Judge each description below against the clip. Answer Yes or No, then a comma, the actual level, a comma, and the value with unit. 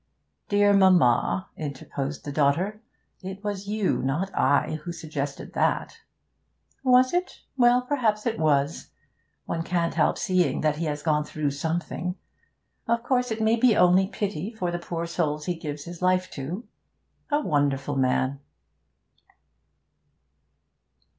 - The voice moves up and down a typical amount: No, wide, 6.0 semitones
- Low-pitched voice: No, medium, 175 Hz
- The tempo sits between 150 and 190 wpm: No, slow, 135 wpm